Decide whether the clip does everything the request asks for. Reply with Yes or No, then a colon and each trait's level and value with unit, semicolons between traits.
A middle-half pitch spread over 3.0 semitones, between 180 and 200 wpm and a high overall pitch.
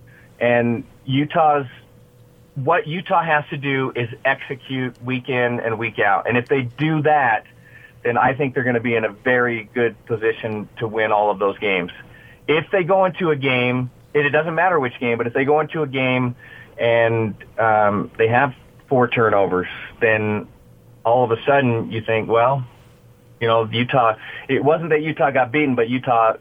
No: average, 3.6 semitones; average, 185 wpm; low, 125 Hz